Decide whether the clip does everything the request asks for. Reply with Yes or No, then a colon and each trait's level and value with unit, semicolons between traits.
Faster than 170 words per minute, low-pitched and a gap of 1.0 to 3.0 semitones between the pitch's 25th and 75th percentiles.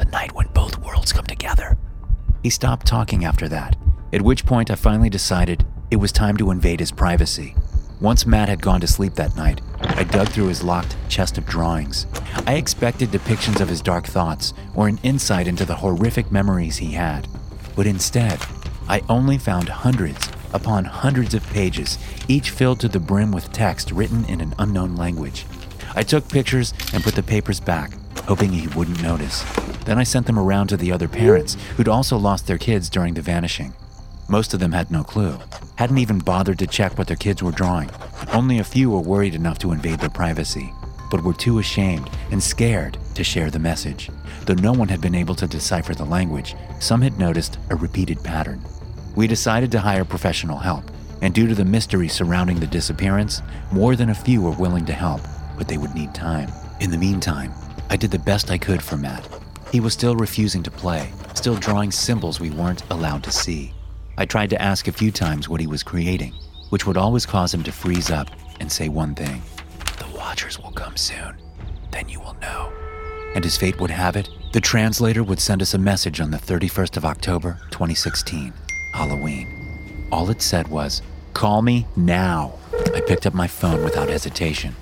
No: average, 195 wpm; very low, 90 Hz; average, 4.0 semitones